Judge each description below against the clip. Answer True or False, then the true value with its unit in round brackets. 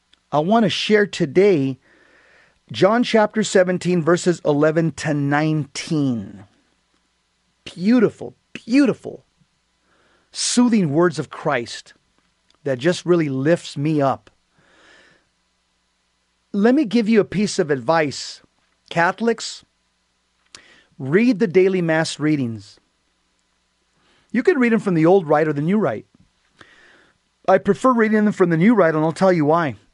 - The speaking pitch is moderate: True (170 Hz)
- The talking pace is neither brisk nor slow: False (125 wpm)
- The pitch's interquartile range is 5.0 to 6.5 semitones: True (5.5 semitones)